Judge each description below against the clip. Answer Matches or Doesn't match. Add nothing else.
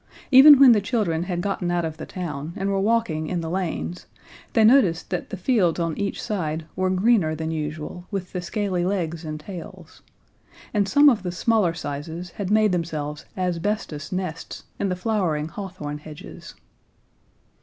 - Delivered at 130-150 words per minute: Doesn't match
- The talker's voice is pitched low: Doesn't match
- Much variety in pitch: Doesn't match